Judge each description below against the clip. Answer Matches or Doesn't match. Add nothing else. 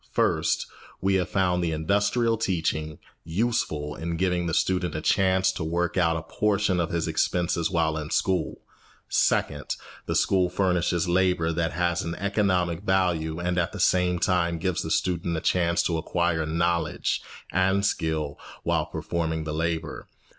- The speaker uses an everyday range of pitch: Doesn't match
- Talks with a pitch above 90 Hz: Doesn't match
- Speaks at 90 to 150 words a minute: Doesn't match